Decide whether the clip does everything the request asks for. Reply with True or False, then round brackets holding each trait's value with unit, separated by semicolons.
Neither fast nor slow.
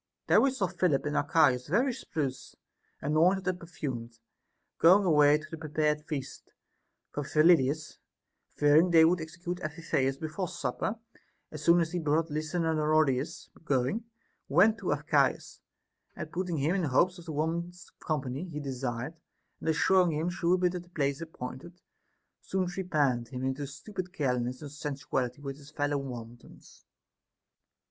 True (155 wpm)